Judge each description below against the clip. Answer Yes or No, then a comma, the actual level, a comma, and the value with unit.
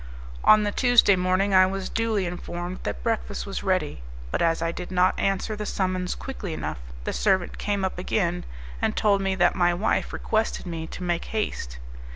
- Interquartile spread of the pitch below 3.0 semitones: Yes, narrow, 2.6 semitones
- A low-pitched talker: No, medium, 185 Hz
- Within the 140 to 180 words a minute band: No, average, 190 wpm